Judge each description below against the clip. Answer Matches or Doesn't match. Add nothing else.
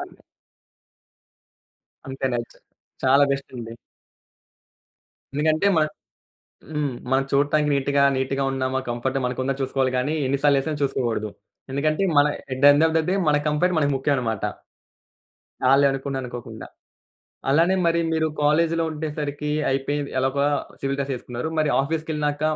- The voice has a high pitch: Doesn't match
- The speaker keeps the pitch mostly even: Matches